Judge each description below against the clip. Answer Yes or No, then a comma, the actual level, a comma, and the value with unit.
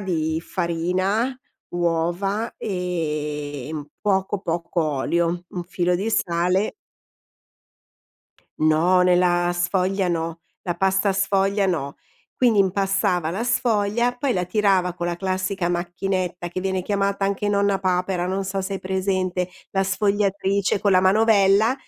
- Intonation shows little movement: Yes, narrow, 2.2 semitones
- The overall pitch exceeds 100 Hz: Yes, medium, 185 Hz